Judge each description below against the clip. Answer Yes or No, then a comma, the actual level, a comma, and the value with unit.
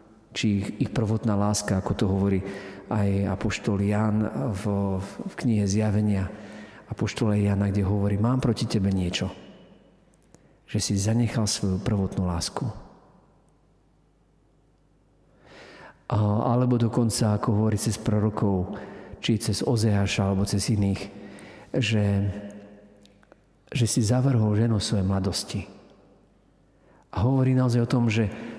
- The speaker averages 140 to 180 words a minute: No, average, 115 wpm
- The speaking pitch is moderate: No, low, 105 Hz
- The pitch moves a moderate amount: No, narrow, 2.2 semitones